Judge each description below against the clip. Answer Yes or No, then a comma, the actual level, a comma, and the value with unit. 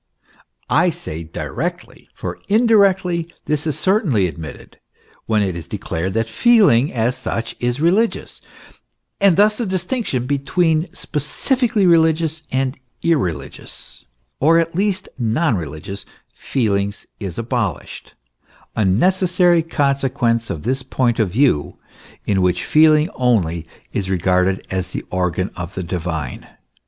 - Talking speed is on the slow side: Yes, slow, 125 wpm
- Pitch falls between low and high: No, low, 130 Hz